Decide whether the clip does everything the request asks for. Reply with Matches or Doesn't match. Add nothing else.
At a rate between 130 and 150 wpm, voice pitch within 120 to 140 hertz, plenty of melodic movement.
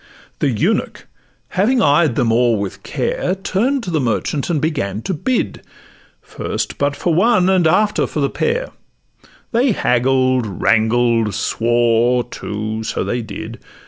Matches